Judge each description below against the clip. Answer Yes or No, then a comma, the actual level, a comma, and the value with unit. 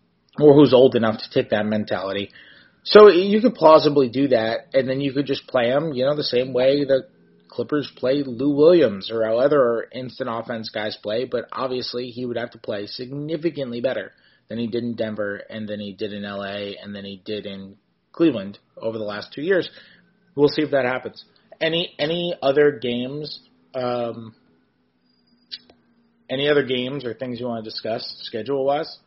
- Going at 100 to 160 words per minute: No, average, 185 wpm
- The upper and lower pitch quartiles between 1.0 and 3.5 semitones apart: No, average, 4.8 semitones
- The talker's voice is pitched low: Yes, low, 125 Hz